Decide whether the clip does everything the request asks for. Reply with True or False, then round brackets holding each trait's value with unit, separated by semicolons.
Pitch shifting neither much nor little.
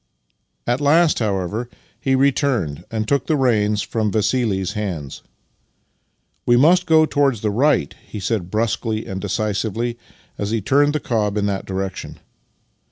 True (4.8 semitones)